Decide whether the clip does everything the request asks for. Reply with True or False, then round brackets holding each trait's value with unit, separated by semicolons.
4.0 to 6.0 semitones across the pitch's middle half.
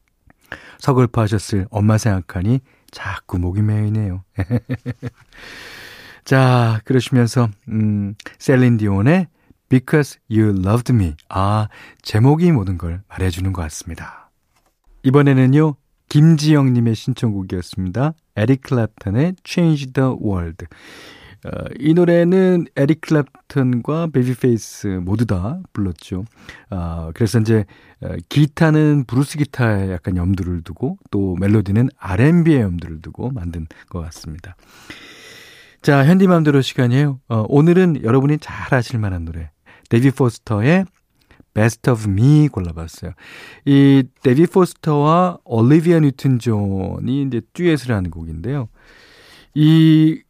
False (6.6 semitones)